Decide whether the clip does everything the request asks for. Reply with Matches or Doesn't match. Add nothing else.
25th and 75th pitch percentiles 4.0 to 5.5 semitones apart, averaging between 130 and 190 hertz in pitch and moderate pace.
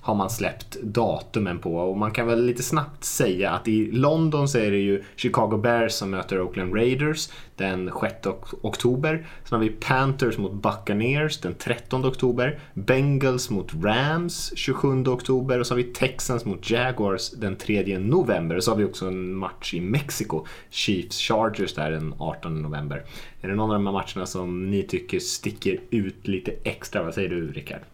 Doesn't match